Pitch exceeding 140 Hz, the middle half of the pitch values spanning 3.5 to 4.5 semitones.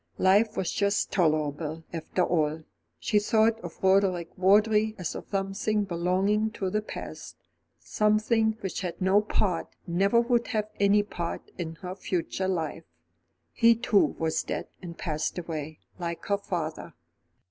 Yes: high, 190 Hz; average, 3.9 semitones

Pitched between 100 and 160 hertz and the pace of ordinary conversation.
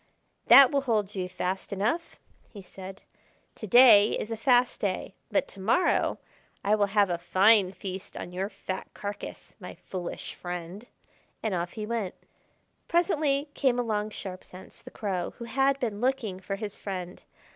No: high, 205 Hz; average, 165 wpm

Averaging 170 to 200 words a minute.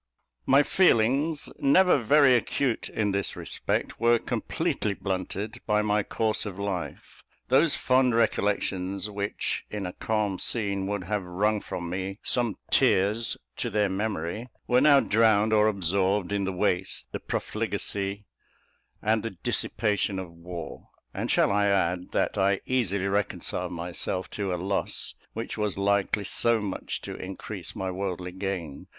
No: average, 145 wpm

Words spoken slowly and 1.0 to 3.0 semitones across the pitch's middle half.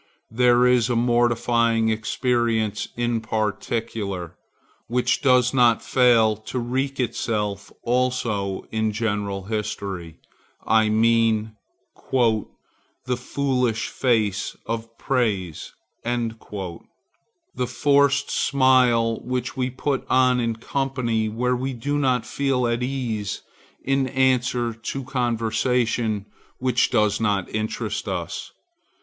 Yes: slow, 105 wpm; narrow, 2.5 semitones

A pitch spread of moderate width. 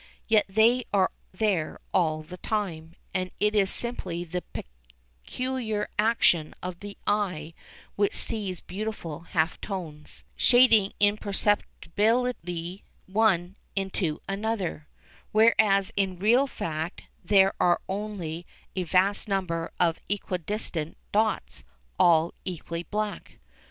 Yes: average, 3.9 semitones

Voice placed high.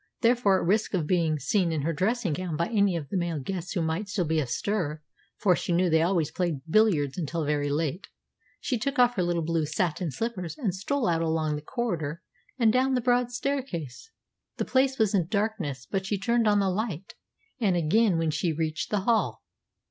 No: medium, 180 Hz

